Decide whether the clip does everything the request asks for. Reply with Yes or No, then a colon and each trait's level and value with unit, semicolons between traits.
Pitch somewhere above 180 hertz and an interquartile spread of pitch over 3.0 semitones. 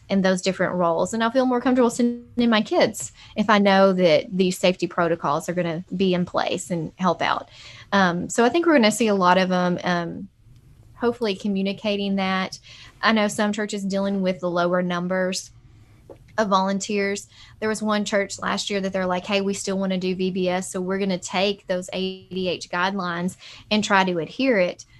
No: high, 190 Hz; average, 2.7 semitones